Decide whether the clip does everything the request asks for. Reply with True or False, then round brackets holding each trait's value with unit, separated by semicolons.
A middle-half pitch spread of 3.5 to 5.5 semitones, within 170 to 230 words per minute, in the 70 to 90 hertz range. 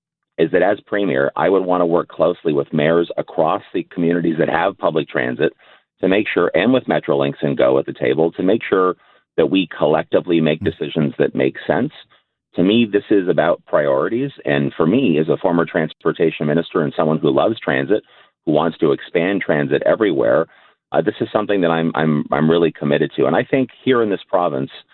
False (3.1 semitones; 205 wpm; 80 Hz)